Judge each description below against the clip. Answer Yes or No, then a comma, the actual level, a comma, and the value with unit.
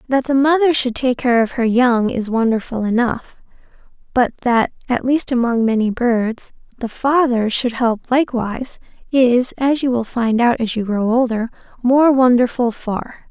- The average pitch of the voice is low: No, high, 245 Hz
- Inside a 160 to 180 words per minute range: Yes, average, 165 wpm